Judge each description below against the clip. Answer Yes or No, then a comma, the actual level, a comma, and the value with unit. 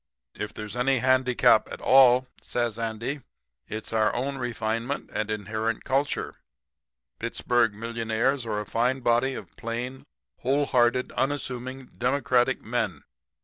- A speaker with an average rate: No, slow, 120 wpm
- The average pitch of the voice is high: No, low, 120 Hz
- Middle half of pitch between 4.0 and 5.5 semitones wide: No, narrow, 2.5 semitones